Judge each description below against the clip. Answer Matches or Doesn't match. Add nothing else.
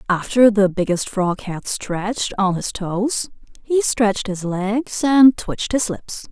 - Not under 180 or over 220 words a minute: Doesn't match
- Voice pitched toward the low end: Doesn't match